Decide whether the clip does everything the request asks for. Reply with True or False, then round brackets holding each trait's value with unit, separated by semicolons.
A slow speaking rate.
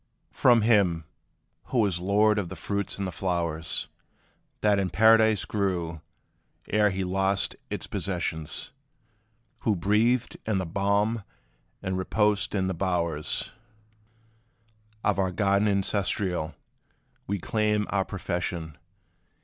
True (115 wpm)